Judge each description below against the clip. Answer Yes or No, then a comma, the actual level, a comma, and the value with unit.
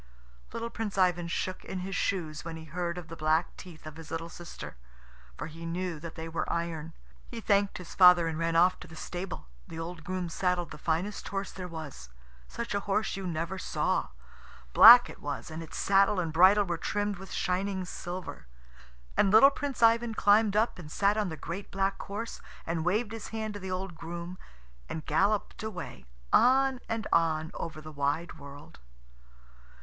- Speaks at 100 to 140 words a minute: No, average, 190 wpm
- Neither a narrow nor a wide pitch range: Yes, average, 3.6 semitones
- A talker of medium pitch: Yes, medium, 180 Hz